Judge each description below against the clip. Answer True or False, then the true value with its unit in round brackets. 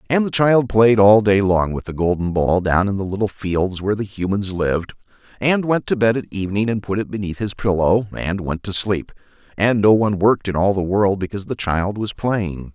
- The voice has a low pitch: True (100 Hz)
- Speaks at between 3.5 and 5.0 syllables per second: False (5.4 syllables/s)